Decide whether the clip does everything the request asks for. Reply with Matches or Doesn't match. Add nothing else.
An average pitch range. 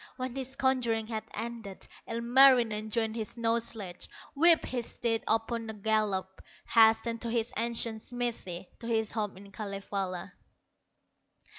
Doesn't match